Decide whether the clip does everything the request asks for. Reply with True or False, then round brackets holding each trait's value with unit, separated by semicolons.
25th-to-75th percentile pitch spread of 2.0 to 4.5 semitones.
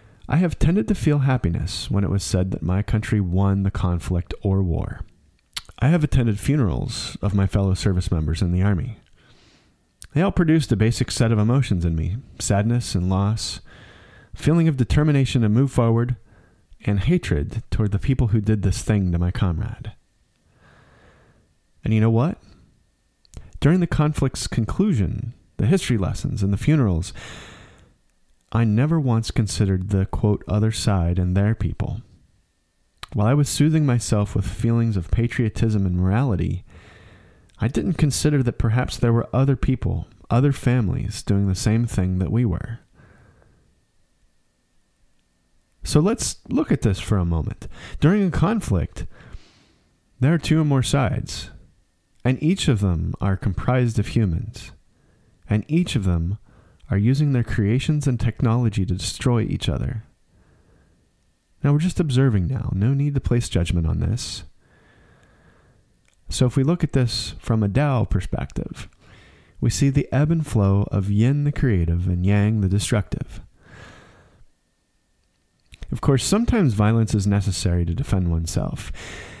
False (5.2 semitones)